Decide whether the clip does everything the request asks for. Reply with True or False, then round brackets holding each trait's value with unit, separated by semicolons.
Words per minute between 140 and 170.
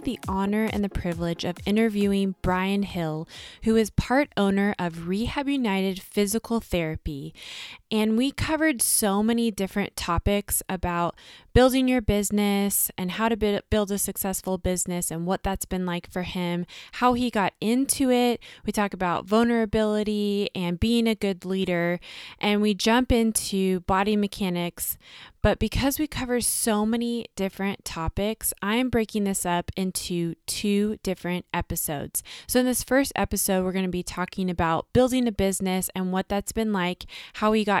True (160 wpm)